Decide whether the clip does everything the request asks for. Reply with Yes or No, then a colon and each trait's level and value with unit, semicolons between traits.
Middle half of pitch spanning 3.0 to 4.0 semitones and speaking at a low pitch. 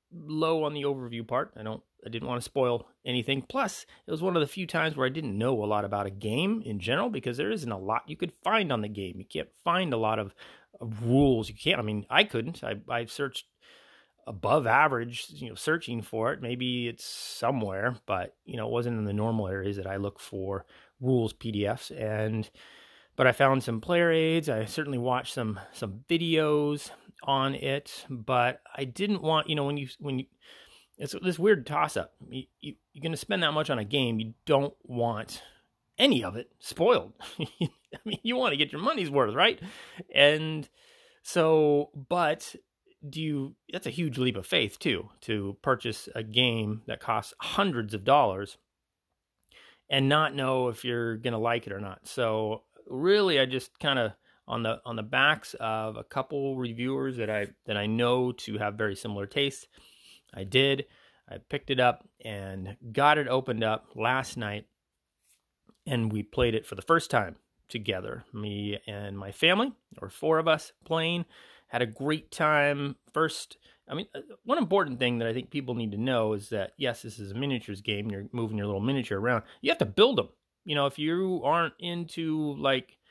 No: wide, 5.4 semitones; low, 125 Hz